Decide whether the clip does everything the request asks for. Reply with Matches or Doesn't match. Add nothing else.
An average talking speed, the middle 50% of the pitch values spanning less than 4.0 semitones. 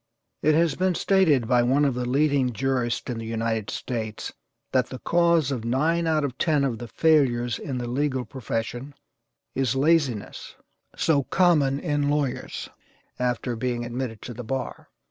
Matches